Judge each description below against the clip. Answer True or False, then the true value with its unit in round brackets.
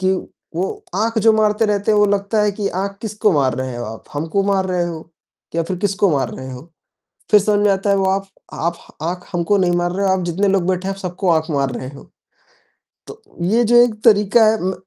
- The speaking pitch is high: True (195 Hz)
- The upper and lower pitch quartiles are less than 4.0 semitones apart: True (3.2 semitones)